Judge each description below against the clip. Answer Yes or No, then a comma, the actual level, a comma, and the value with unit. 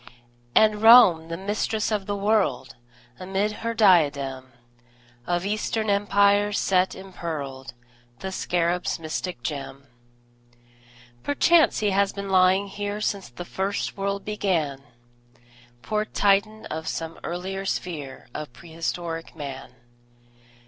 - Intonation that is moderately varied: Yes, average, 4.0 semitones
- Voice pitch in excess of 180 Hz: Yes, high, 190 Hz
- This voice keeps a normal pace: No, slow, 115 wpm